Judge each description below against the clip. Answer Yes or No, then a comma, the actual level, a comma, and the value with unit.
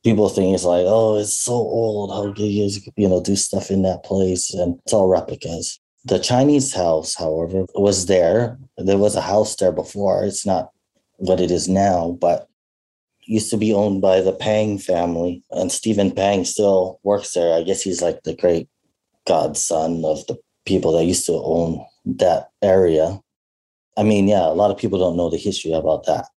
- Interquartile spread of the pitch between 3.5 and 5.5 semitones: No, average, 3.1 semitones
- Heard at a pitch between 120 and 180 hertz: No, very low, 95 Hz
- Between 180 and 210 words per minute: Yes, average, 195 wpm